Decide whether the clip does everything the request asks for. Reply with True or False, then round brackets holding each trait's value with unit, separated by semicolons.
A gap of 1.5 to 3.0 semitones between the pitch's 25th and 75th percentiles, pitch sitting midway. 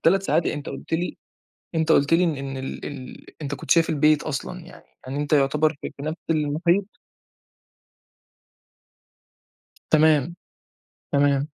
True (2.6 semitones; 150 Hz)